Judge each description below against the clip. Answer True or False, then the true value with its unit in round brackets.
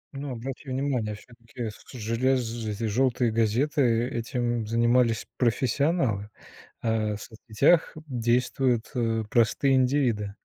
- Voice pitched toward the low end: True (120 Hz)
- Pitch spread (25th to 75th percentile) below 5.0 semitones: True (2.7 semitones)